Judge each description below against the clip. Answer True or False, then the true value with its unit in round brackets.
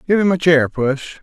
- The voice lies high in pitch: False (160 Hz)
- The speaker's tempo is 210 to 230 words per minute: False (245 wpm)